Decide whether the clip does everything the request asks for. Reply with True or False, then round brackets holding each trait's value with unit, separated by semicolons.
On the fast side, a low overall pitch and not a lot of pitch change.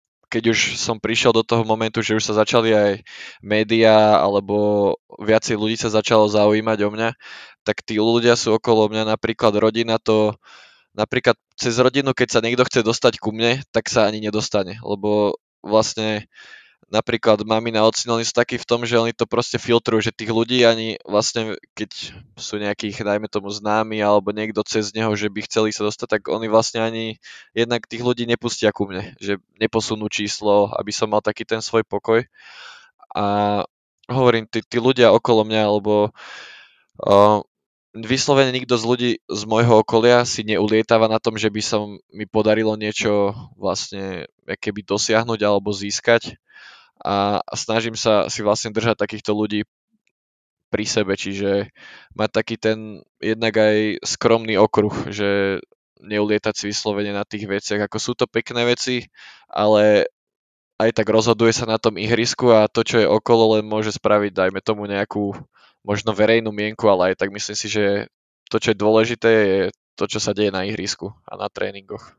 True (170 wpm; 110 Hz; 1.6 semitones)